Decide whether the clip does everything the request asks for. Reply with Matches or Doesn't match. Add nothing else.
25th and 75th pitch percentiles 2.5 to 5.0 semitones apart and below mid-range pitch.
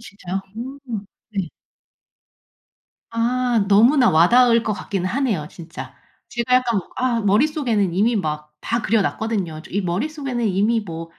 Doesn't match